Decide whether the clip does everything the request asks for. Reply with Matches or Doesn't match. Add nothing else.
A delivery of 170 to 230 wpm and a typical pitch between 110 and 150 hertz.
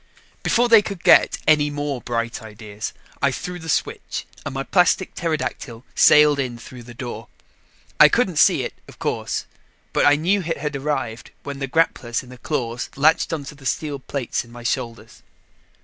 Matches